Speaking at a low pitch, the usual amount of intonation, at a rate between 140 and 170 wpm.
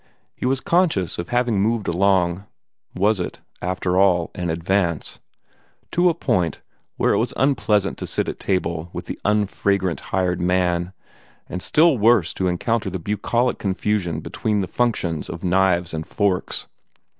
Yes: very low, 95 Hz; average, 3.5 semitones; average, 155 wpm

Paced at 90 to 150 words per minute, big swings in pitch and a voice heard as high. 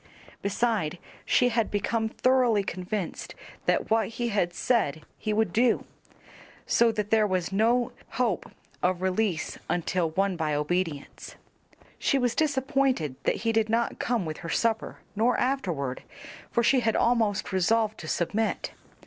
No: average, 145 wpm; average, 4.5 semitones; high, 215 Hz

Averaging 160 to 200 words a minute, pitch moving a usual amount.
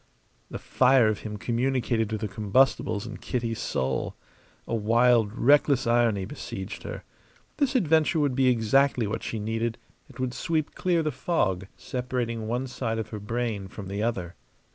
Yes: average, 165 wpm; average, 3.5 semitones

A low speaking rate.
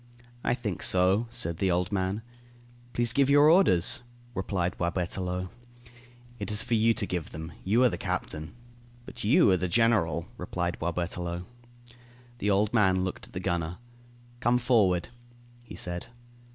No: average, 150 wpm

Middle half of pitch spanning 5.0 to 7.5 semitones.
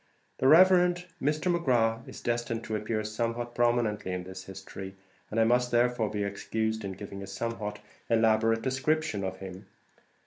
No: average, 3.1 semitones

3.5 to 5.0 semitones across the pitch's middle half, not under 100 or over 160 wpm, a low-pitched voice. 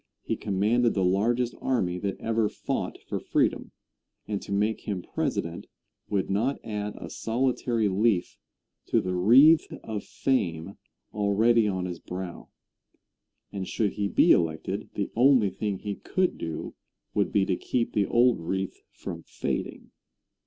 Yes: average, 3.8 semitones; average, 145 wpm; low, 105 Hz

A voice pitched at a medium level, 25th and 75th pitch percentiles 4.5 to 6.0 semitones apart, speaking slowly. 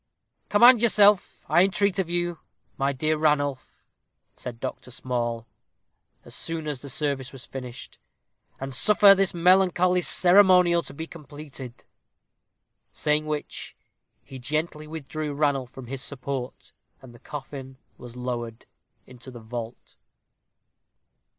Yes: medium, 145 Hz; average, 5.2 semitones; slow, 125 wpm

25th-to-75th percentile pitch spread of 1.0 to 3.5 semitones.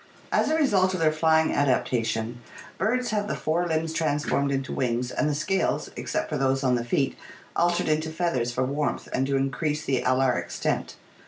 No: average, 3.9 semitones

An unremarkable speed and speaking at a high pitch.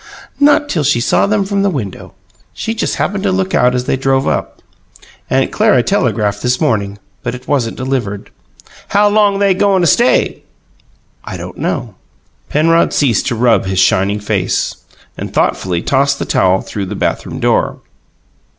No: average, 170 wpm; low, 135 Hz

